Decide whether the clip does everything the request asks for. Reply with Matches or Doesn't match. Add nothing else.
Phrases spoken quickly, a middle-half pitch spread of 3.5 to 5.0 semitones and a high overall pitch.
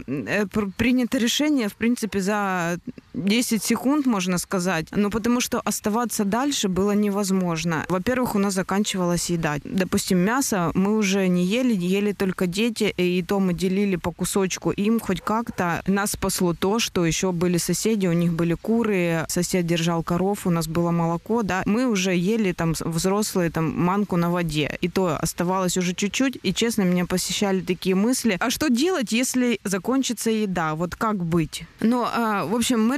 Matches